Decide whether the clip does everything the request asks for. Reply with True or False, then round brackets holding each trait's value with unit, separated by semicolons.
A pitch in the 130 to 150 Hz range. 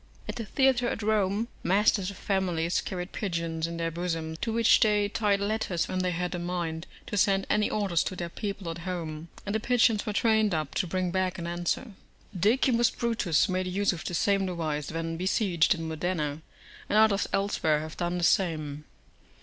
False (185 Hz)